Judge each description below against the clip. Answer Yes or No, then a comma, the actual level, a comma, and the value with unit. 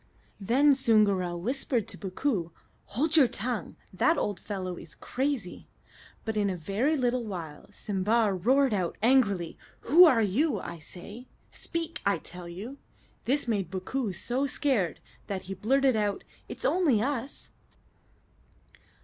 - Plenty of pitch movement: Yes, wide, 6.1 semitones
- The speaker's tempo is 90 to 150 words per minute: Yes, average, 140 wpm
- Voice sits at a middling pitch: No, high, 220 Hz